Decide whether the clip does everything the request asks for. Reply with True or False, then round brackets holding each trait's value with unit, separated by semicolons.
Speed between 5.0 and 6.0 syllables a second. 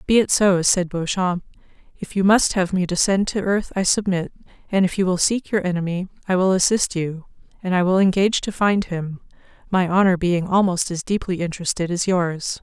True (5.3 syllables/s)